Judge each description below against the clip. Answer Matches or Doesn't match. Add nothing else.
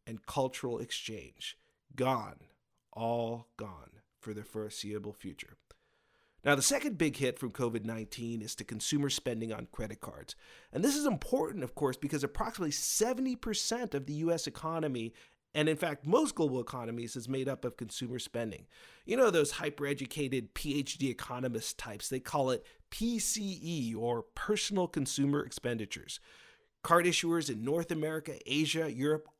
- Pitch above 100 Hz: Matches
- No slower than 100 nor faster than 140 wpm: Doesn't match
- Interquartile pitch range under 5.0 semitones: Doesn't match